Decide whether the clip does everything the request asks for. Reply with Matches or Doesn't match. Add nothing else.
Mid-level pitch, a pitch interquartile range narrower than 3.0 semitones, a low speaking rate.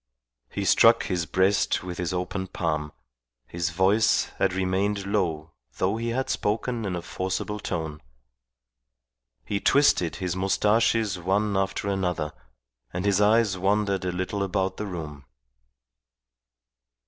Doesn't match